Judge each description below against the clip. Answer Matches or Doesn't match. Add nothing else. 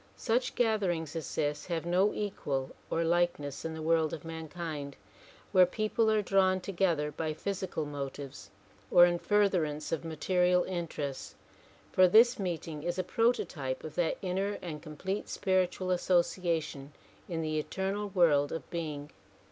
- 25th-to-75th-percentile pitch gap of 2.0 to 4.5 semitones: Matches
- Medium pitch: Matches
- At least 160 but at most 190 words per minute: Doesn't match